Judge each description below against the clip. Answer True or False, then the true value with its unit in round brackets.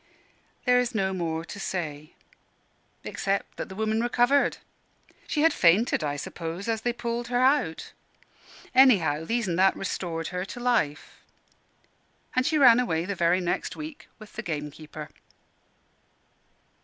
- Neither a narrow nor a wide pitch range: False (6.7 semitones)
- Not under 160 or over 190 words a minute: False (145 wpm)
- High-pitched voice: True (195 Hz)